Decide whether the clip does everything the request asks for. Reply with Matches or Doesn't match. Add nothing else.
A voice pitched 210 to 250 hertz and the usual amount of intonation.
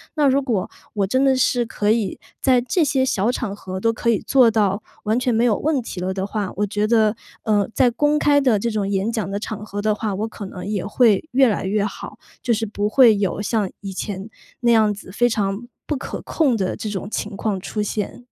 Matches